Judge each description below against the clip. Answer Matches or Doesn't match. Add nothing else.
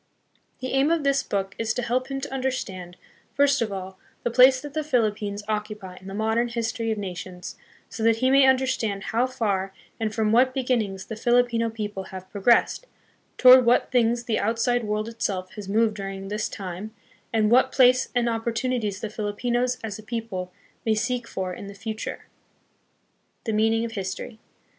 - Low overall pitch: Doesn't match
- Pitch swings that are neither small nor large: Matches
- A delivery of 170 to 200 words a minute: Matches